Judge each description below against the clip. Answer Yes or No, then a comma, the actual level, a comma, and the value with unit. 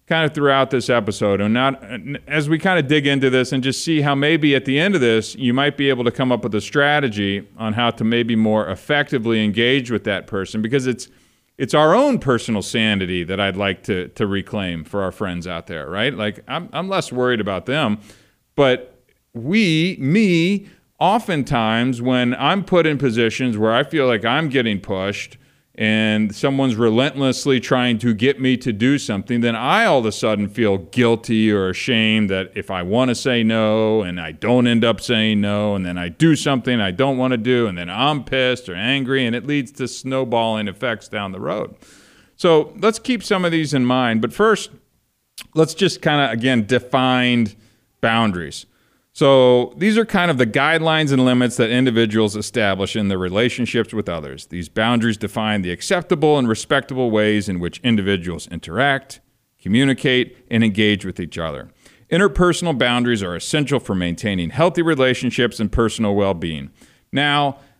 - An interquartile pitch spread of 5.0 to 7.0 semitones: No, average, 4.6 semitones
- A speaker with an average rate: Yes, average, 185 wpm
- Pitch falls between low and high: No, low, 125 Hz